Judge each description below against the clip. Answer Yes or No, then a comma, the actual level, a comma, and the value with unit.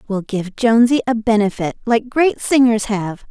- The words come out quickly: No, average, 165 wpm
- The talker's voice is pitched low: No, high, 225 Hz